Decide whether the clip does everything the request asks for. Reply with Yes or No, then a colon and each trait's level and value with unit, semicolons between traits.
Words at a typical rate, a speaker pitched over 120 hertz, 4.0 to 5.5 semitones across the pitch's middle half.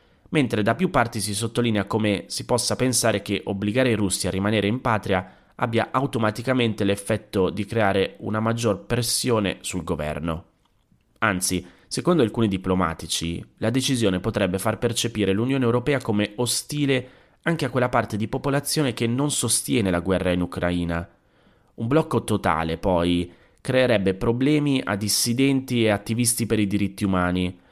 No: average, 145 wpm; low, 110 Hz; average, 4.4 semitones